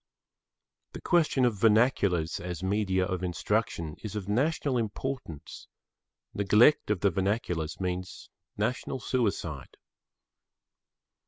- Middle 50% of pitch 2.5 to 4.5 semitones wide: No, average, 5.1 semitones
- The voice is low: Yes, low, 100 Hz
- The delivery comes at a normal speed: No, slow, 100 wpm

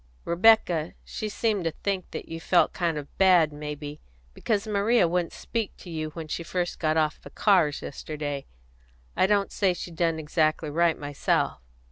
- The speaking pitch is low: No, medium, 170 Hz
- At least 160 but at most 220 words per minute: Yes, average, 180 wpm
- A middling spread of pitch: Yes, average, 3.8 semitones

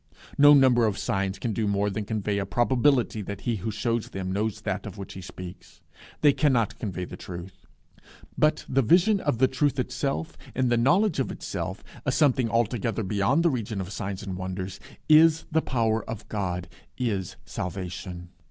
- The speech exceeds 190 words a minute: No, average, 180 wpm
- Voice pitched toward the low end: Yes, low, 110 Hz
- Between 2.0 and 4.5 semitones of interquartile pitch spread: No, average, 5.3 semitones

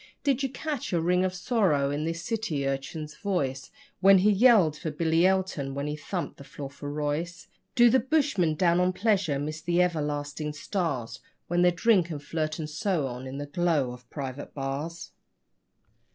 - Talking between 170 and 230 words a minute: Yes, average, 180 wpm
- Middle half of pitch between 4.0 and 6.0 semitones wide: Yes, average, 4.4 semitones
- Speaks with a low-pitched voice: No, medium, 165 Hz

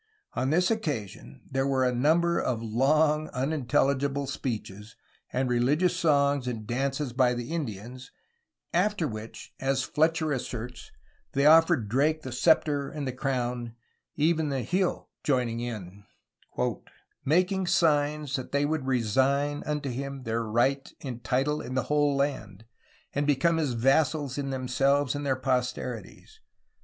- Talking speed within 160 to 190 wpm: No, slow, 135 wpm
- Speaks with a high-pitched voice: No, low, 135 Hz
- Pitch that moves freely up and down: No, average, 3.3 semitones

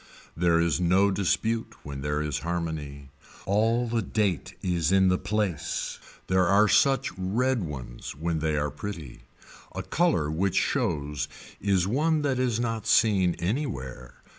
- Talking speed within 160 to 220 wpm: No, average, 145 wpm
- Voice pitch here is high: No, very low, 90 Hz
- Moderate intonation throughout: No, wide, 6.3 semitones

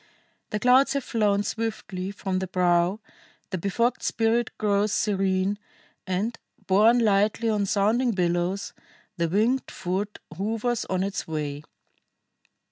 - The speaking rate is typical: No, slow, 125 wpm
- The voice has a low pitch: No, high, 200 Hz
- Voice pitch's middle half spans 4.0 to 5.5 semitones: No, average, 3.2 semitones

